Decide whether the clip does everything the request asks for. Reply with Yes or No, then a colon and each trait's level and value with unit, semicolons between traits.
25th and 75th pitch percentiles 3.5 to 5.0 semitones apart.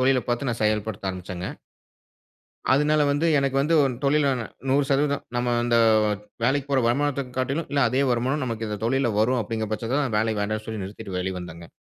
Yes: average, 4.3 semitones